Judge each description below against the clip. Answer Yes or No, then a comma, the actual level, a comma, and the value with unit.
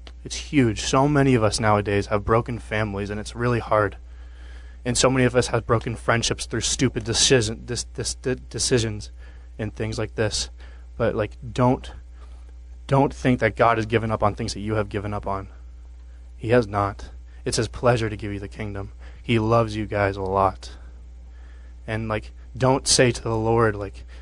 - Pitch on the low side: Yes, low, 105 Hz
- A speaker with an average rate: Yes, average, 180 wpm